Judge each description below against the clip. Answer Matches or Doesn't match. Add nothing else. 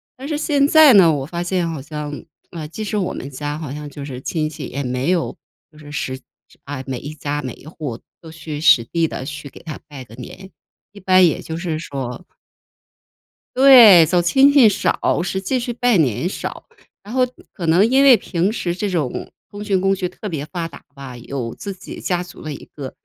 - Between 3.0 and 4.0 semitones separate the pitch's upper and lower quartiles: Doesn't match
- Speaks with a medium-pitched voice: Matches